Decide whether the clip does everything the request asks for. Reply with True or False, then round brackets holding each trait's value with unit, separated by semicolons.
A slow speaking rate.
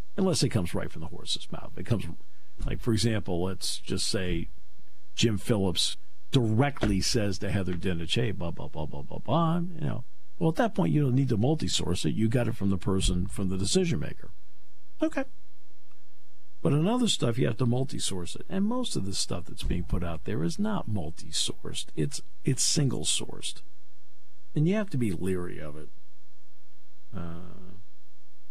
False (190 wpm)